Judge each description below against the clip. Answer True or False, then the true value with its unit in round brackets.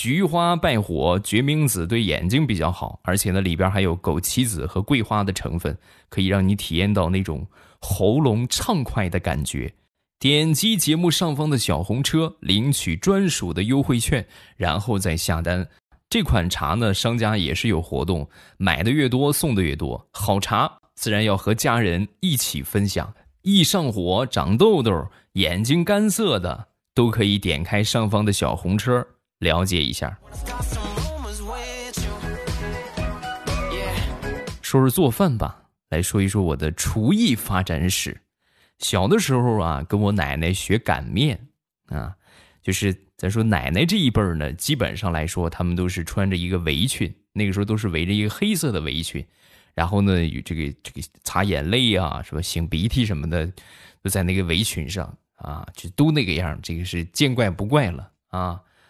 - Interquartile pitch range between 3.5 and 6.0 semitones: True (5.6 semitones)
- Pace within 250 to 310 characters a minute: False (240 characters per minute)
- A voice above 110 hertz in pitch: False (100 Hz)